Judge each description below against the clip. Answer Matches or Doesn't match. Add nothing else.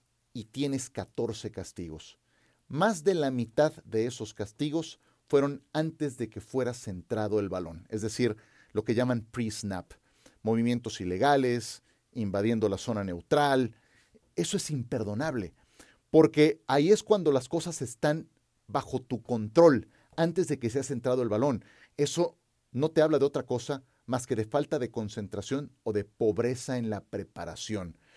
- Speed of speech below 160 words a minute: Matches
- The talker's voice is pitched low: Matches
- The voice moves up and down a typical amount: Matches